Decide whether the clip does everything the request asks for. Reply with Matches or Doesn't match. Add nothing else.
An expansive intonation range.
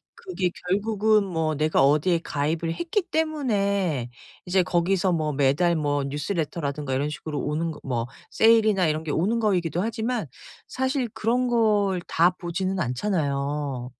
Matches